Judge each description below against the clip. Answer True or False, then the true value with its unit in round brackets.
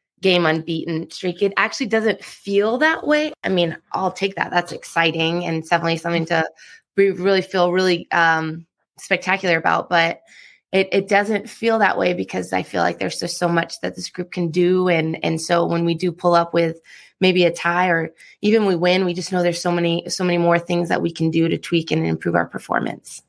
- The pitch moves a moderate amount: False (2.1 semitones)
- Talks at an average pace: False (215 wpm)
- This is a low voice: False (175 Hz)